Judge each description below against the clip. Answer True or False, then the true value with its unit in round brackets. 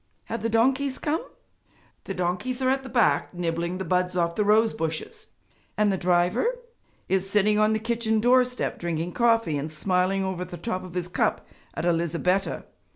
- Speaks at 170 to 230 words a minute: True (180 wpm)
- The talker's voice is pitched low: False (195 Hz)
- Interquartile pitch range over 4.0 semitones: True (4.6 semitones)